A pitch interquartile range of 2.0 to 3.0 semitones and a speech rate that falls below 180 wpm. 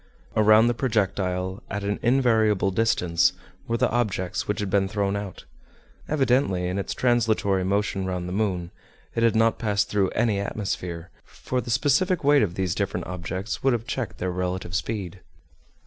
No: average, 3.7 semitones; average, 165 wpm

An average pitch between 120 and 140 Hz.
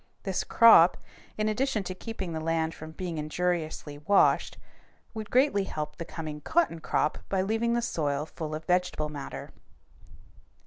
No: medium, 175 Hz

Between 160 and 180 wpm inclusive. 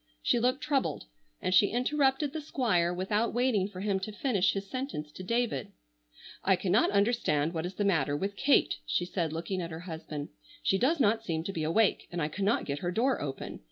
No: fast, 205 wpm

